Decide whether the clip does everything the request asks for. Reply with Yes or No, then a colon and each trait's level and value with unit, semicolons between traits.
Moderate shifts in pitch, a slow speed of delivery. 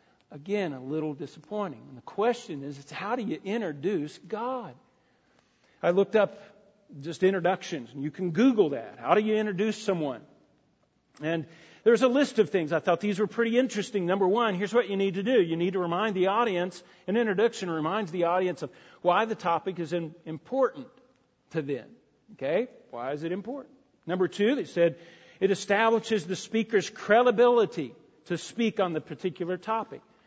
No: average, 4.6 semitones; average, 175 wpm